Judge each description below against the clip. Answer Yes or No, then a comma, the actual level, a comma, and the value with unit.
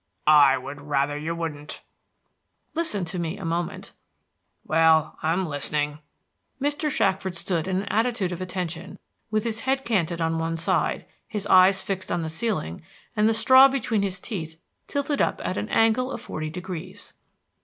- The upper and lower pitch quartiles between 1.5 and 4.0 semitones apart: No, average, 5.1 semitones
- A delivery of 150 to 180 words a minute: Yes, average, 165 wpm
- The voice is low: No, medium, 180 Hz